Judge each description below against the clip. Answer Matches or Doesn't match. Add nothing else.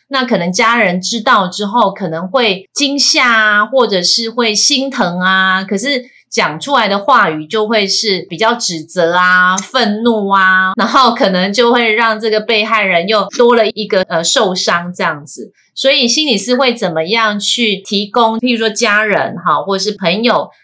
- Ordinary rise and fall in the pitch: Matches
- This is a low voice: Doesn't match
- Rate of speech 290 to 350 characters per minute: Doesn't match